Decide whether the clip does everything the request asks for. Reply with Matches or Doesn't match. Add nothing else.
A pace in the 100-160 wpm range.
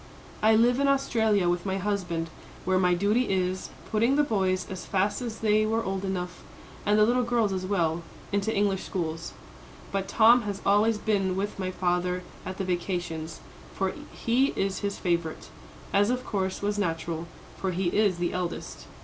Doesn't match